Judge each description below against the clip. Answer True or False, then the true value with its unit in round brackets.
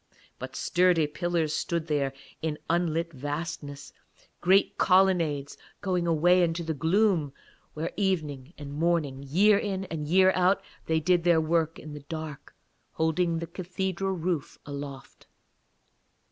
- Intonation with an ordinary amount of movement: True (3.2 semitones)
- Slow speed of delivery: True (130 wpm)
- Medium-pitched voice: True (165 Hz)